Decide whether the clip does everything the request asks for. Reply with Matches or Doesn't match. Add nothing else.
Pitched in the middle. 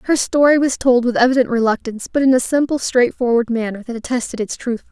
Doesn't match